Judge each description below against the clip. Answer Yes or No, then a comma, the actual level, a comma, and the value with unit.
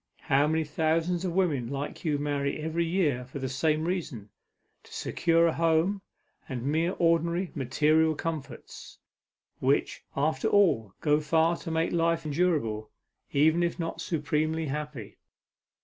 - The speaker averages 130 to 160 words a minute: Yes, average, 140 wpm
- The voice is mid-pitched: Yes, medium, 155 Hz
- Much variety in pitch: No, average, 2.8 semitones